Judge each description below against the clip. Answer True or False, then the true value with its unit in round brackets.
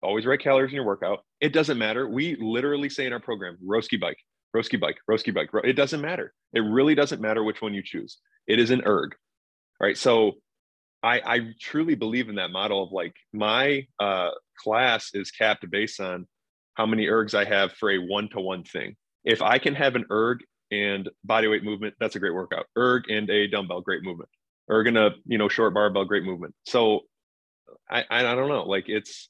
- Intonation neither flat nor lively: True (4.4 semitones)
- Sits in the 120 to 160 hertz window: False (110 Hz)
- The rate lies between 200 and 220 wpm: True (205 wpm)